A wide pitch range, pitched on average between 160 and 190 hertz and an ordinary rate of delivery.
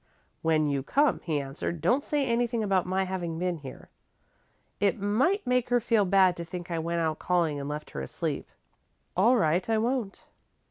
Yes: wide, 6.1 semitones; medium, 185 Hz; average, 185 wpm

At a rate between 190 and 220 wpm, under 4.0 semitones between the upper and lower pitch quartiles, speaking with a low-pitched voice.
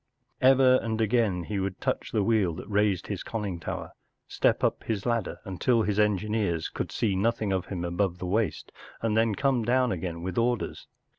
Yes: fast, 205 wpm; average, 3.5 semitones; low, 105 Hz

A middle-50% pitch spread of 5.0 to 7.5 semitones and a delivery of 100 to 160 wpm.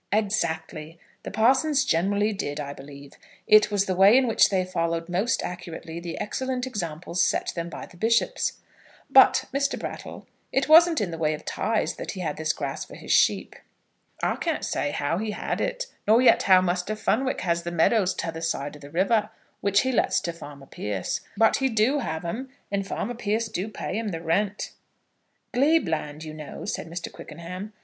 No: average, 5.3 semitones; average, 190 wpm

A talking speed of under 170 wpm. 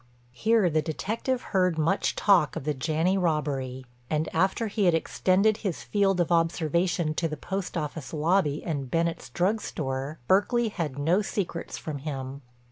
Yes: average, 160 wpm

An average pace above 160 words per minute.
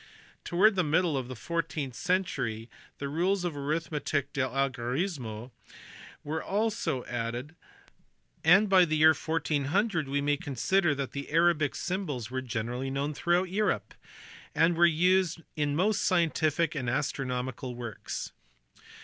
No: slow, 135 wpm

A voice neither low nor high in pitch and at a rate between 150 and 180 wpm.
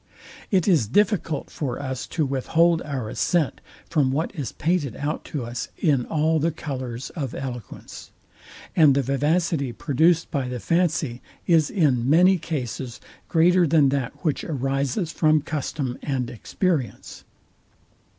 No: medium, 145 Hz; average, 140 wpm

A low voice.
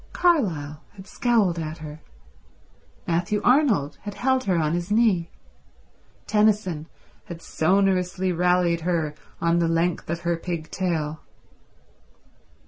No: medium, 175 Hz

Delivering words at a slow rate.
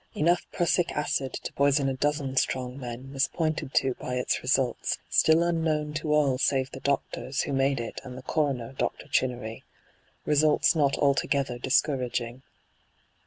No: average, 160 wpm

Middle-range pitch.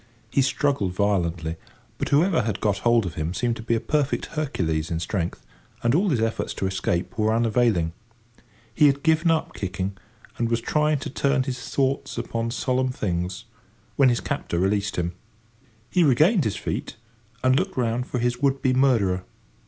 No: low, 115 Hz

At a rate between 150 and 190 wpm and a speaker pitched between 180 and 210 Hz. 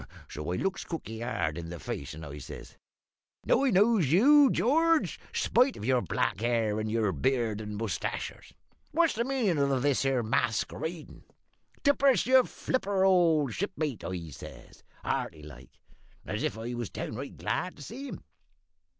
No: average, 170 wpm; low, 135 Hz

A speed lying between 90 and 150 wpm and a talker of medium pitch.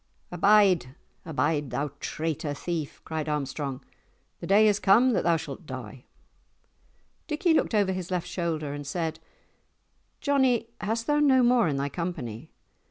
Yes: average, 145 wpm; medium, 175 Hz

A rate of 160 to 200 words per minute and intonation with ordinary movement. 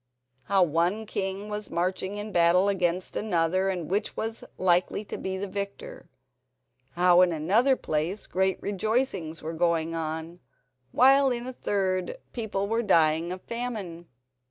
No: average, 145 wpm; average, 3.4 semitones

